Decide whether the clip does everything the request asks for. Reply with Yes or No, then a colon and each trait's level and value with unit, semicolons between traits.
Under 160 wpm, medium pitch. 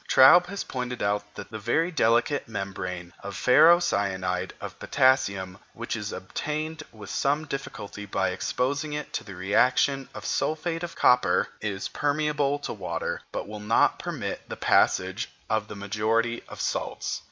No: average, 150 wpm; low, 115 Hz